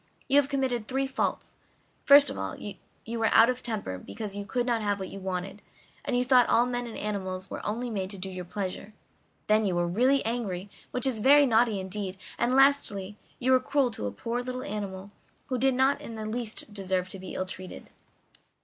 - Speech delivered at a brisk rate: Yes, fast, 210 wpm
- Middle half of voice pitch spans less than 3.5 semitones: No, average, 4.6 semitones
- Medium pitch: No, high, 220 Hz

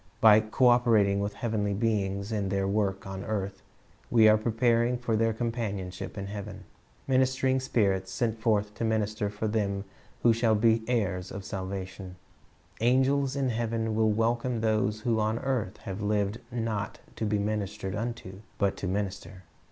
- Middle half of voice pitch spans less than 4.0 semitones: Yes, narrow, 2.6 semitones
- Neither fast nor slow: Yes, average, 160 wpm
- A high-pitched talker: No, low, 110 Hz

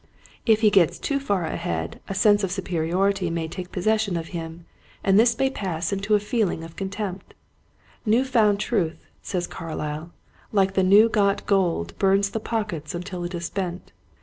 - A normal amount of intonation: Yes, average, 3.4 semitones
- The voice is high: Yes, high, 195 Hz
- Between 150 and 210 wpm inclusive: Yes, average, 175 wpm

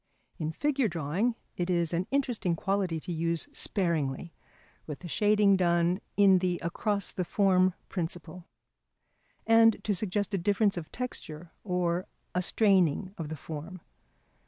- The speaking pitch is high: No, medium, 180 Hz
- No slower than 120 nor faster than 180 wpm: Yes, average, 140 wpm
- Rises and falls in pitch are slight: No, average, 3.2 semitones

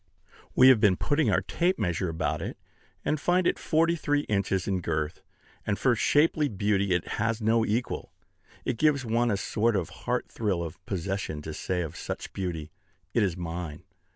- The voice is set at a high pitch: No, low, 100 Hz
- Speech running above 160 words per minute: Yes, average, 180 wpm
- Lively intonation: Yes, wide, 6.1 semitones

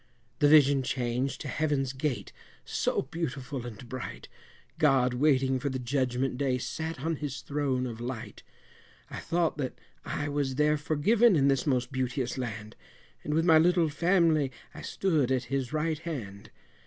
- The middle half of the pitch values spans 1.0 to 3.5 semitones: Yes, average, 3.2 semitones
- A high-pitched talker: No, low, 135 Hz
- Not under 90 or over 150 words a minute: No, average, 160 wpm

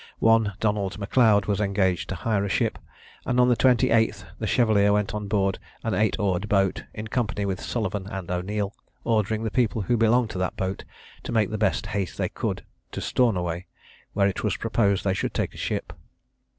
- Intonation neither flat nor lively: No, narrow, 2.3 semitones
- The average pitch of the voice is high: No, low, 105 Hz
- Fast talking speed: No, average, 190 wpm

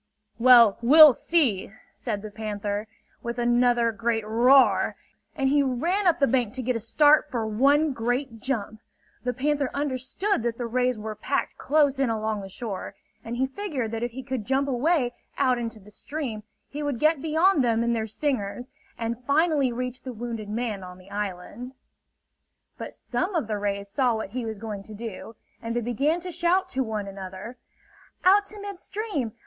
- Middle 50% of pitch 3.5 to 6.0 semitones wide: Yes, average, 4.3 semitones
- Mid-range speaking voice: No, high, 245 Hz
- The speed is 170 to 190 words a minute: Yes, average, 185 wpm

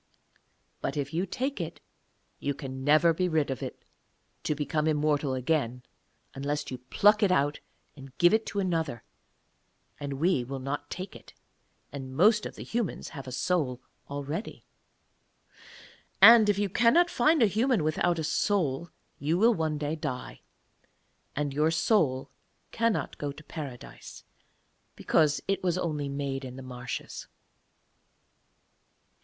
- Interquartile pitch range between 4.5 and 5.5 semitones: Yes, average, 5.0 semitones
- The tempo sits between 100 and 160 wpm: Yes, average, 145 wpm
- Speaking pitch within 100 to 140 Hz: No, medium, 155 Hz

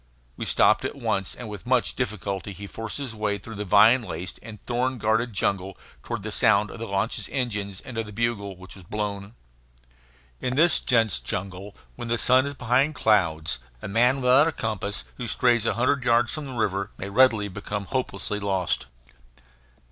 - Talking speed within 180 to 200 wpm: Yes, average, 185 wpm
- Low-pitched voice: Yes, low, 110 Hz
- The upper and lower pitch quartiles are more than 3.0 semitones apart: Yes, average, 3.7 semitones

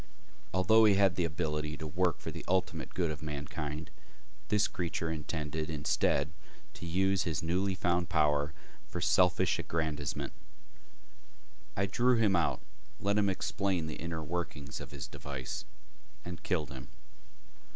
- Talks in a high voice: No, very low, 85 Hz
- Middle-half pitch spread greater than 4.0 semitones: No, average, 3.7 semitones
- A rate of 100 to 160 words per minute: Yes, average, 140 wpm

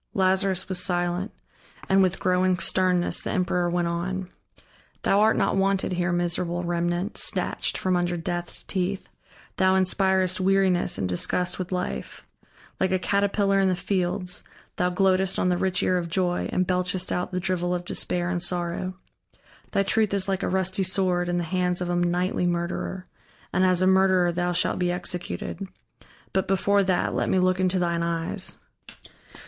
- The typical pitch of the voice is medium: Yes, medium, 180 Hz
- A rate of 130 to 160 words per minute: No, average, 170 wpm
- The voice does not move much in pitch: Yes, narrow, 1.3 semitones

